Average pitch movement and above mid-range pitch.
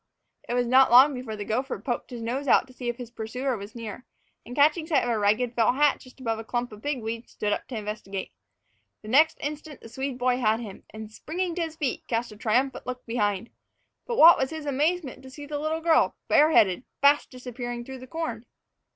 Yes: average, 4.1 semitones; very high, 250 Hz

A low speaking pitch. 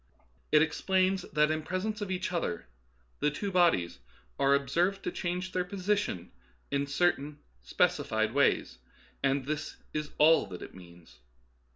No: medium, 155 Hz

